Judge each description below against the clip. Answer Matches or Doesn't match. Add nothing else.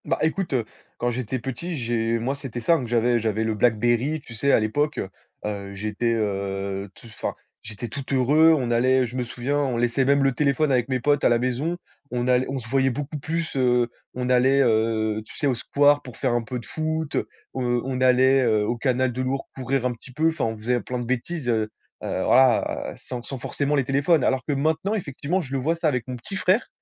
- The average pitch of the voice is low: Matches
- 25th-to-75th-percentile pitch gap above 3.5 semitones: Doesn't match